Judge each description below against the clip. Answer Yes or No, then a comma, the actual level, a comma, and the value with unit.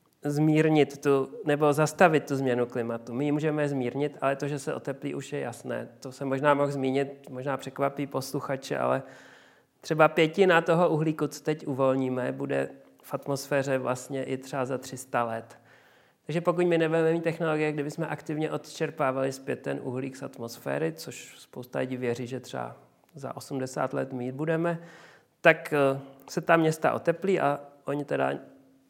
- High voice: No, medium, 140 Hz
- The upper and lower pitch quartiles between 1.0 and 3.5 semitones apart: Yes, average, 2.9 semitones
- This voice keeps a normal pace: Yes, average, 160 wpm